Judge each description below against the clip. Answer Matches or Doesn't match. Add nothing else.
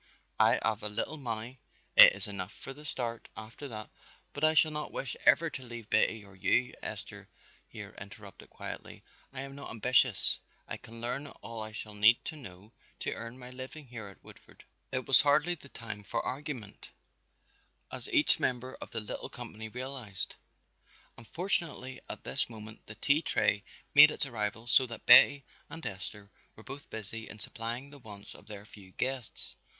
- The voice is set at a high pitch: Doesn't match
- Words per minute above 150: Matches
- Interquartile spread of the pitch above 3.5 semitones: Matches